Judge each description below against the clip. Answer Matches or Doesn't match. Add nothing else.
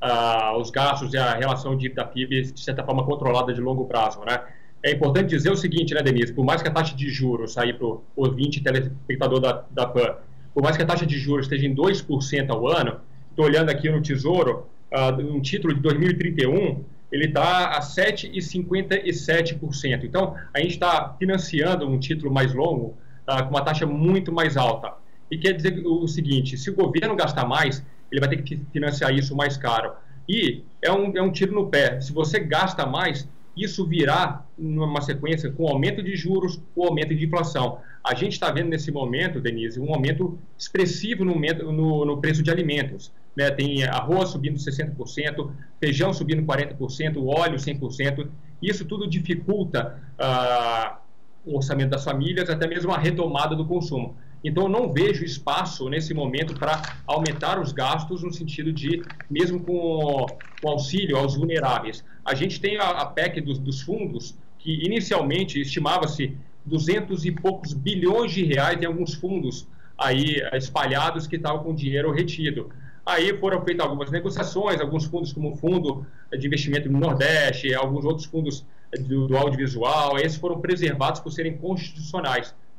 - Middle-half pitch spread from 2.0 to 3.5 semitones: Doesn't match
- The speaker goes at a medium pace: Matches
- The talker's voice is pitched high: Doesn't match